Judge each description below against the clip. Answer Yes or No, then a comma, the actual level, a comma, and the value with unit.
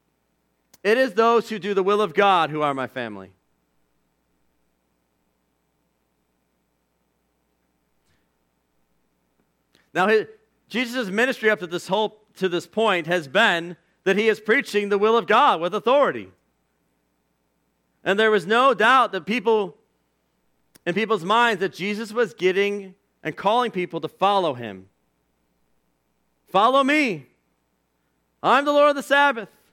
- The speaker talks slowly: Yes, slow, 125 wpm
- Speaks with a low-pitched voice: No, medium, 160 Hz